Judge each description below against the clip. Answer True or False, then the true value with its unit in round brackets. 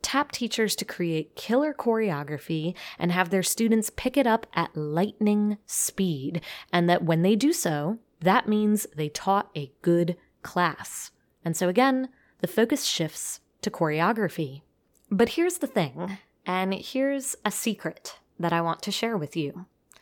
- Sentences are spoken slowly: False (155 wpm)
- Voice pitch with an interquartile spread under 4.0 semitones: False (5.1 semitones)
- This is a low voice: False (195 Hz)